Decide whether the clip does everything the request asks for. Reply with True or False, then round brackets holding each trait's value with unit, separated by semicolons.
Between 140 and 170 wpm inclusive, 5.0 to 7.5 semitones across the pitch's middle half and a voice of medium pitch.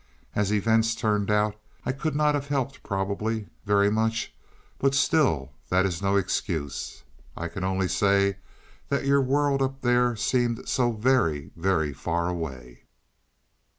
False (145 wpm; 5.4 semitones; 105 Hz)